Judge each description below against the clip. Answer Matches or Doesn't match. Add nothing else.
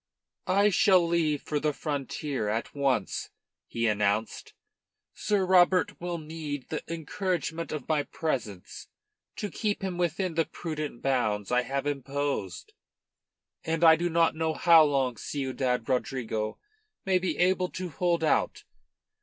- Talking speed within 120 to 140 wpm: Matches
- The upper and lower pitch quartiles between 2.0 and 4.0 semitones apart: Doesn't match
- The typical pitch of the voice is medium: Matches